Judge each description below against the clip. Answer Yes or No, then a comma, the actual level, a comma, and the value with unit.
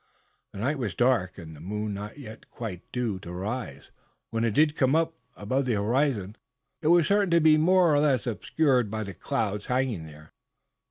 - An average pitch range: No, wide, 6.3 semitones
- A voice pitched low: Yes, low, 115 Hz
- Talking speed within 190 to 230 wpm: Yes, average, 195 wpm